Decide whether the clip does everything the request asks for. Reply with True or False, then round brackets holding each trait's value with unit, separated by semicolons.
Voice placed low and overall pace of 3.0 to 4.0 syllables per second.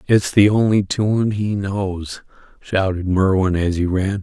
True (100 Hz; 3.7 syllables/s)